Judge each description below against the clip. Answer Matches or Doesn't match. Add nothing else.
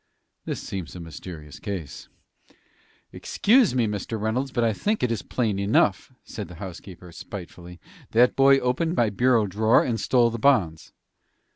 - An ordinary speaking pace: Matches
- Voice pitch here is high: Doesn't match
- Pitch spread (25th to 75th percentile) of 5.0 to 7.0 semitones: Matches